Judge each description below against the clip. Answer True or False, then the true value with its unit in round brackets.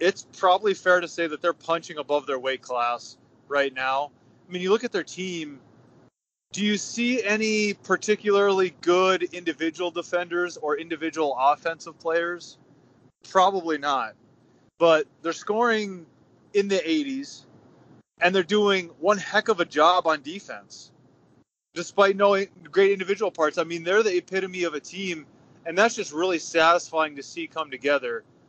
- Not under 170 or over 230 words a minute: False (155 wpm)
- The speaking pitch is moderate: True (175 Hz)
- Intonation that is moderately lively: True (3.8 semitones)